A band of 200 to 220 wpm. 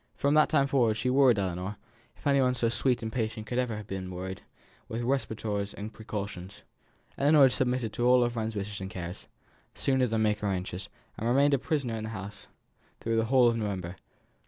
Yes: fast, 205 wpm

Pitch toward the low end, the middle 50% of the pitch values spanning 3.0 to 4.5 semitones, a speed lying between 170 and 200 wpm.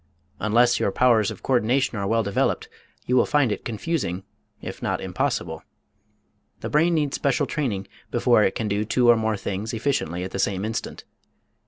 Yes: low, 115 Hz; average, 4.0 semitones; average, 175 wpm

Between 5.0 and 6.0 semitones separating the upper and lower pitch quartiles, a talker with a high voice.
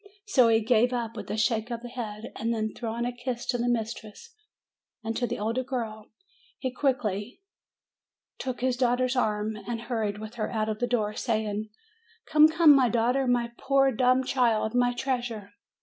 No: narrow, 2.5 semitones; high, 235 Hz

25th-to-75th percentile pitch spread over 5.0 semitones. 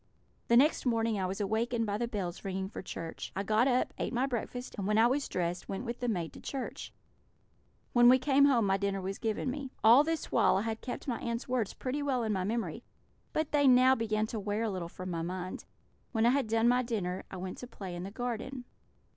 No: average, 4.3 semitones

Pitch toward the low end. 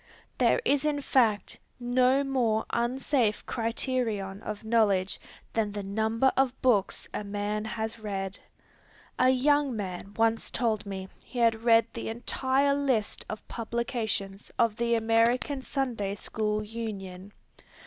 No: high, 225 Hz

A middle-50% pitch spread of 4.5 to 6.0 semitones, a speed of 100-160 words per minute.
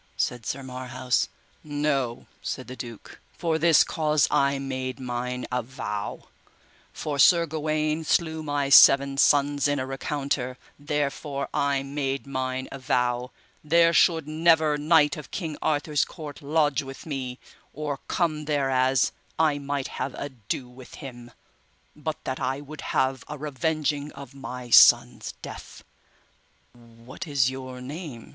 No: average, 2.7 semitones; slow, 135 wpm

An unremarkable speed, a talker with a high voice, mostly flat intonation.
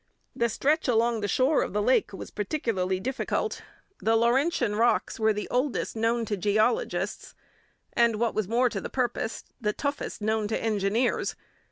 No: average, 165 wpm; high, 230 Hz; average, 3.1 semitones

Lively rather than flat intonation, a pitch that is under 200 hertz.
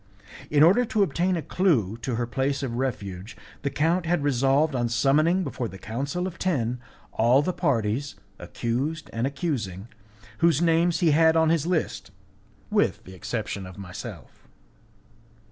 Yes: wide, 5.9 semitones; medium, 140 Hz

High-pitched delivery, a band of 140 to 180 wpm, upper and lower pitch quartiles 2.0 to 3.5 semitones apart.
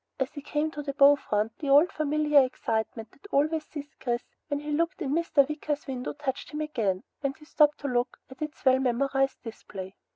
No: very high, 280 Hz; fast, 205 wpm; average, 2.8 semitones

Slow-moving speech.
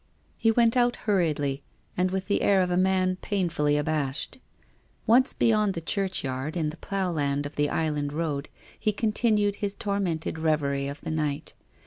No: average, 170 wpm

